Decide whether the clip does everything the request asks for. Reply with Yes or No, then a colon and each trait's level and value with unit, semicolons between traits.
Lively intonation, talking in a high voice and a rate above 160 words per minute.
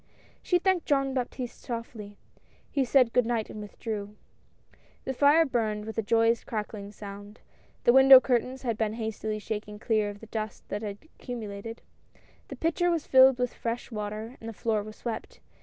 No: average, 3.5 semitones; high, 225 Hz; average, 175 wpm